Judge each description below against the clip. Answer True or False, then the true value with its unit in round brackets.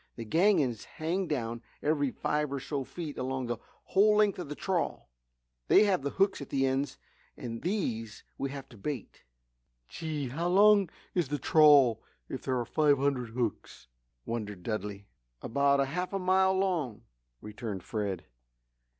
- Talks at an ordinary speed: True (160 wpm)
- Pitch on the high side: False (140 Hz)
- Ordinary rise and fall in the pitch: False (6.7 semitones)